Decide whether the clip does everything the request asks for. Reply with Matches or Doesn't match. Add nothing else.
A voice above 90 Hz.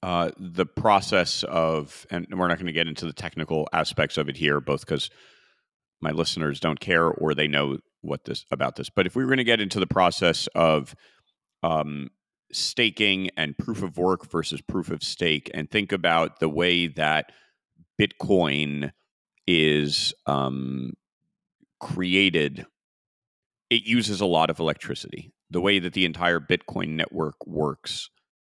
Doesn't match